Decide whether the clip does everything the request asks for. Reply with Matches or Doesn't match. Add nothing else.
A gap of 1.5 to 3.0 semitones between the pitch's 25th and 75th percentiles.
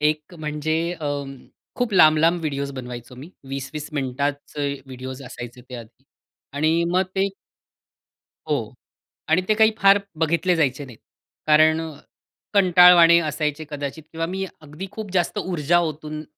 Doesn't match